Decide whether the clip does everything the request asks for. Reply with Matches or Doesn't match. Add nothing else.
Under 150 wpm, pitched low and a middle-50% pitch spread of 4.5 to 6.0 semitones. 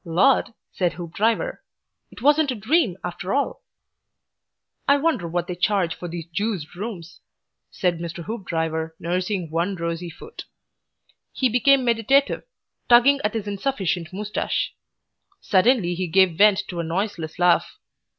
Doesn't match